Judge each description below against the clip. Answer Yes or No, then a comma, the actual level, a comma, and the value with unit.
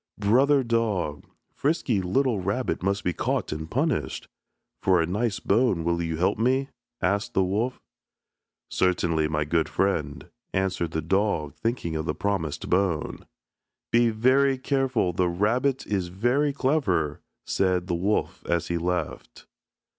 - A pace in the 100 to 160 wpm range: Yes, average, 140 wpm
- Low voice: Yes, very low, 95 Hz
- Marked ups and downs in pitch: Yes, wide, 6.0 semitones